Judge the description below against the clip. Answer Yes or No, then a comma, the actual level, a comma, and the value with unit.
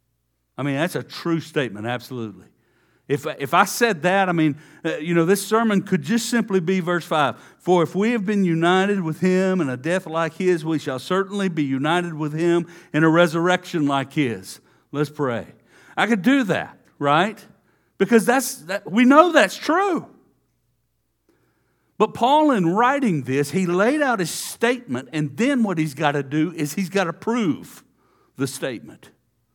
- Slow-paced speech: No, average, 180 wpm